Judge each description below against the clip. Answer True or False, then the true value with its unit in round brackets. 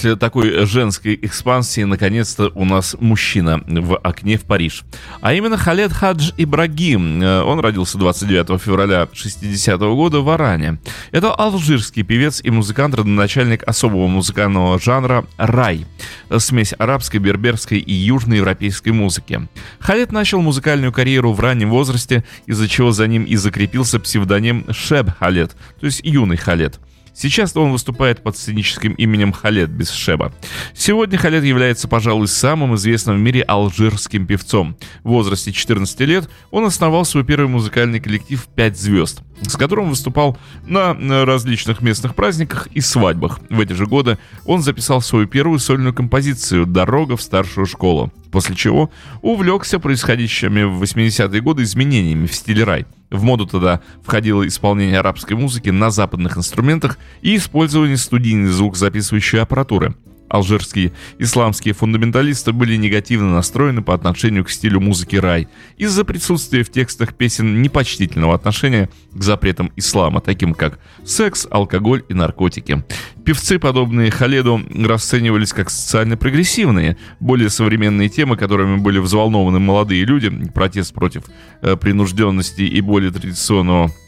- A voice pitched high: False (110 Hz)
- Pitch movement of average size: True (4.9 semitones)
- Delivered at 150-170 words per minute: False (135 wpm)